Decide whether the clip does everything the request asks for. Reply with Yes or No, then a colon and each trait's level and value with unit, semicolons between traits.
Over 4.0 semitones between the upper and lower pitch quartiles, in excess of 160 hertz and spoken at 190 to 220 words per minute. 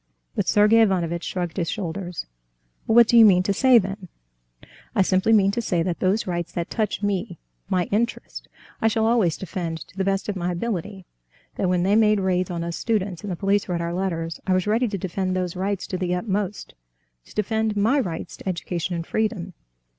No: average, 3.0 semitones; high, 190 Hz; fast, 205 wpm